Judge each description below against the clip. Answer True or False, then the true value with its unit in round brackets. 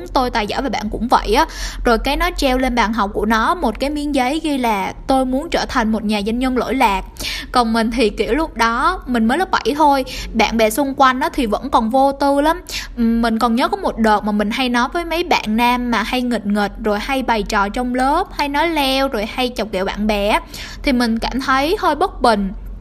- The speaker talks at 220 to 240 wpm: False (250 wpm)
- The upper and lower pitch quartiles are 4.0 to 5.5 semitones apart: True (4.3 semitones)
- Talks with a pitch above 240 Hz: True (250 Hz)